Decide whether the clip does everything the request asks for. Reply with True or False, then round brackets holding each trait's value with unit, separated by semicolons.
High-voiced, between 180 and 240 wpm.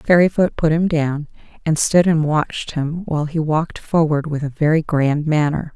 False (155 Hz; 190 wpm)